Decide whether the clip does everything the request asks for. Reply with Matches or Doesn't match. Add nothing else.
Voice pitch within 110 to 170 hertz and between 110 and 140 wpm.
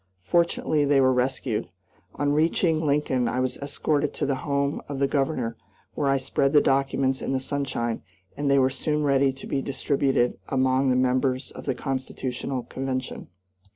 Doesn't match